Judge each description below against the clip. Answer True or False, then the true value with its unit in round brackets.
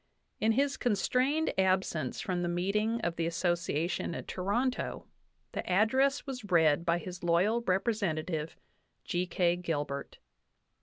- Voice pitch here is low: False (185 Hz)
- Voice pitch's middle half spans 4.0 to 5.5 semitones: True (4.8 semitones)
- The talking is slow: True (125 wpm)